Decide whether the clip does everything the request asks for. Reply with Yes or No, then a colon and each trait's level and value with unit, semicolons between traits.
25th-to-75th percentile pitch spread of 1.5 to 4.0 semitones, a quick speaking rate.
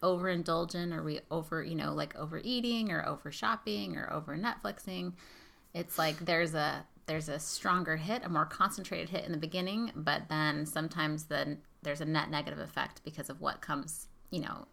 No: average, 3.1 semitones; average, 180 wpm